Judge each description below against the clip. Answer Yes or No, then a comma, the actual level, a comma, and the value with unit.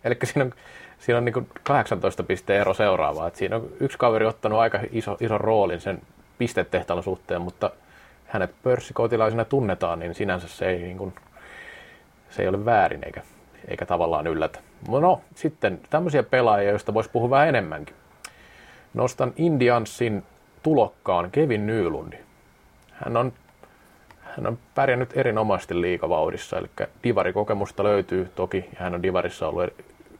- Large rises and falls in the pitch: No, average, 3.5 semitones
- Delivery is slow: No, average, 140 wpm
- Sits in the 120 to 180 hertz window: No, low, 110 Hz